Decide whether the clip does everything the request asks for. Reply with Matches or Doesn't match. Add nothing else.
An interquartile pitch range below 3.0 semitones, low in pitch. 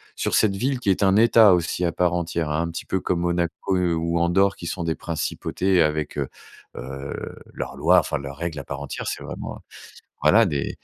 Doesn't match